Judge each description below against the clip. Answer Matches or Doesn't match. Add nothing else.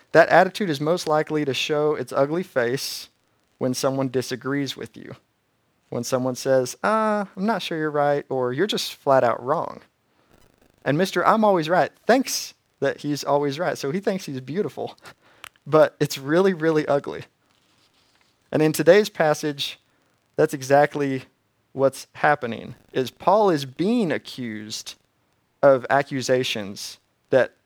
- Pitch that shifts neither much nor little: Matches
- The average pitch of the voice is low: Doesn't match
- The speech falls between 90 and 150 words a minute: Matches